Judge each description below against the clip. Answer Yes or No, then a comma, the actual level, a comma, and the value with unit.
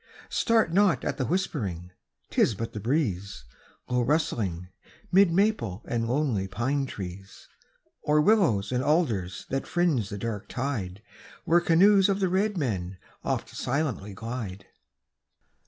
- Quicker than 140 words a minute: No, slow, 135 wpm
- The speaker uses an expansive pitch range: Yes, wide, 8.9 semitones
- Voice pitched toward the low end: Yes, low, 125 Hz